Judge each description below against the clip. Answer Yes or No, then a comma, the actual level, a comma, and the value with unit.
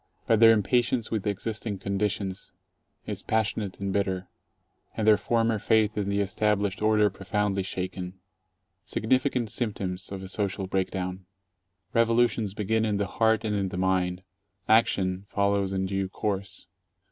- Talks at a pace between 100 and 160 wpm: Yes, average, 140 wpm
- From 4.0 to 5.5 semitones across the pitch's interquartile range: No, narrow, 2.4 semitones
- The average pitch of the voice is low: Yes, low, 100 Hz